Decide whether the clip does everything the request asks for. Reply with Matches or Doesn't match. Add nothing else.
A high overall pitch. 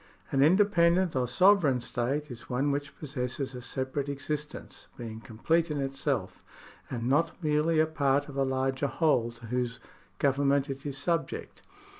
Doesn't match